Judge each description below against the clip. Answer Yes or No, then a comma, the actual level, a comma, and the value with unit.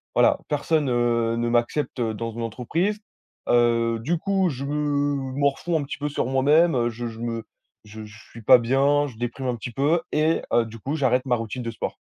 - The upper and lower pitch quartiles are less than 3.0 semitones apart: No, average, 3.8 semitones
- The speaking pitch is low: Yes, low, 125 Hz